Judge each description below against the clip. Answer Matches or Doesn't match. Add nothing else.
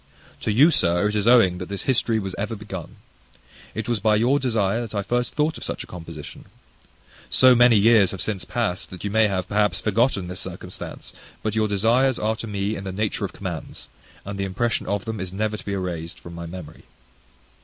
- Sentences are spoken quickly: Matches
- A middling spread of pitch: Matches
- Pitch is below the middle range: Matches